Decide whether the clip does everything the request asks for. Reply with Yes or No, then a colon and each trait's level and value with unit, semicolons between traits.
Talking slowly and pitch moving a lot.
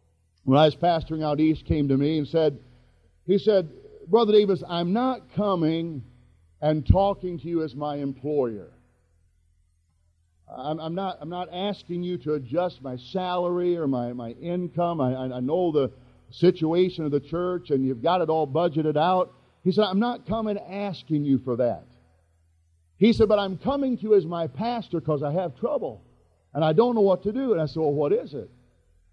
No: average, 190 wpm; wide, 6.2 semitones